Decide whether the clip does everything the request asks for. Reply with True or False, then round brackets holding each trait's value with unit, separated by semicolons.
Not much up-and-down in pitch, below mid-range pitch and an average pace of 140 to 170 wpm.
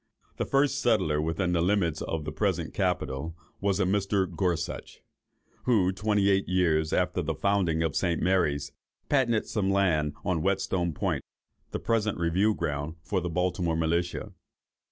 False (3.4 semitones; 90 Hz; 155 wpm)